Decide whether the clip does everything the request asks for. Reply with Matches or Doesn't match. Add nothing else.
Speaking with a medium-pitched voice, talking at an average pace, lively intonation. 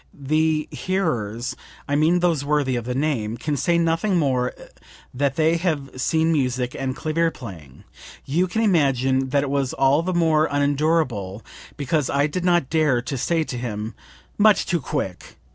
Doesn't match